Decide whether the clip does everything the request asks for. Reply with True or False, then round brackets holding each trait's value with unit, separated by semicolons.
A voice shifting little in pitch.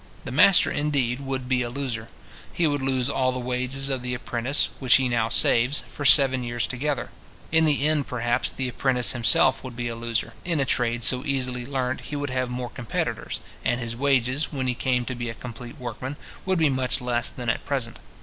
True (2.3 semitones)